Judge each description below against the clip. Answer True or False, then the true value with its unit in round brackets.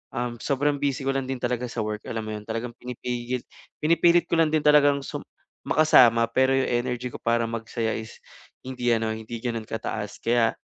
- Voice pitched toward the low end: True (120 Hz)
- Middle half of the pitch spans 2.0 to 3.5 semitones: True (2.9 semitones)